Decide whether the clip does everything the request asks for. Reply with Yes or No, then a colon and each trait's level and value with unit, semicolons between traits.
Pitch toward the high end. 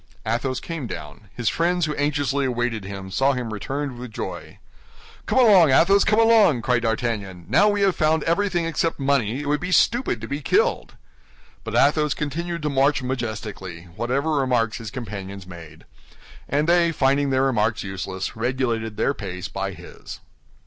No: low, 130 Hz